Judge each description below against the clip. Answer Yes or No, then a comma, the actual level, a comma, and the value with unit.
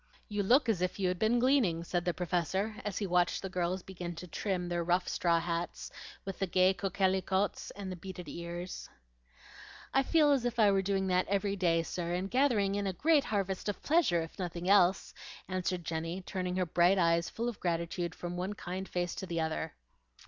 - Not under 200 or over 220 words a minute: Yes, fast, 205 wpm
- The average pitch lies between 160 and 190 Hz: Yes, medium, 185 Hz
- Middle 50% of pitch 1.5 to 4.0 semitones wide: Yes, narrow, 2.4 semitones